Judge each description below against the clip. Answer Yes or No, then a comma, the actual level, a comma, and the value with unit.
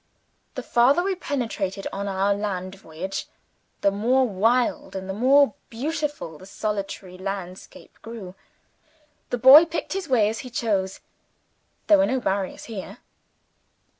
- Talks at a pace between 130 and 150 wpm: Yes, slow, 135 wpm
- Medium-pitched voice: No, high, 215 Hz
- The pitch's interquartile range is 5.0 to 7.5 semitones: Yes, average, 5.3 semitones